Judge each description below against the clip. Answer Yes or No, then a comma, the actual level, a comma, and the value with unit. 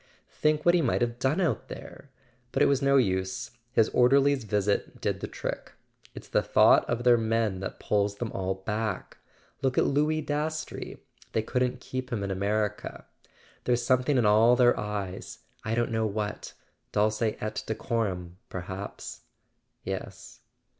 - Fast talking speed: No, average, 160 wpm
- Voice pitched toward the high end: No, low, 115 Hz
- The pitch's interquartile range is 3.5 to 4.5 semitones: Yes, average, 3.9 semitones